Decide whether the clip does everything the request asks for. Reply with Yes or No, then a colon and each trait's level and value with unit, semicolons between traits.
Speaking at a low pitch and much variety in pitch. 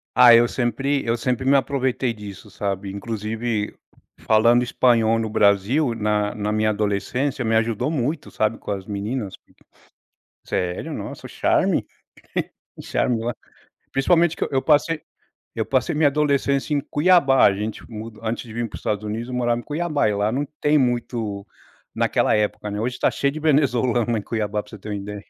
No: low, 115 Hz; average, 4.2 semitones